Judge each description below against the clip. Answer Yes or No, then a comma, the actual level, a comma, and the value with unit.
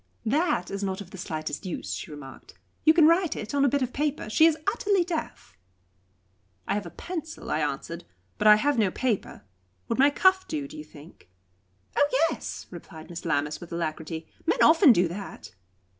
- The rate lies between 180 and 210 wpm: Yes, average, 190 wpm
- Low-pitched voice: No, high, 220 Hz